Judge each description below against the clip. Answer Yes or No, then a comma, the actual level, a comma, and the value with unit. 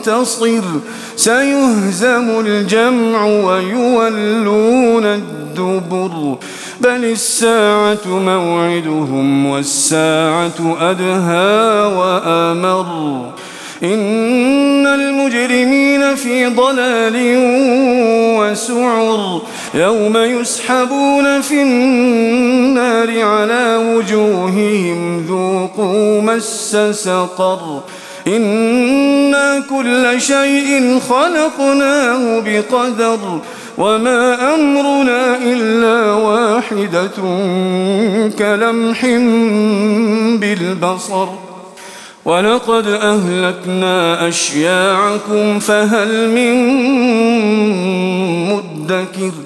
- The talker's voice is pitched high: Yes, high, 220 Hz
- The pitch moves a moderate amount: Yes, average, 4.6 semitones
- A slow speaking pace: Yes, slow, 50 wpm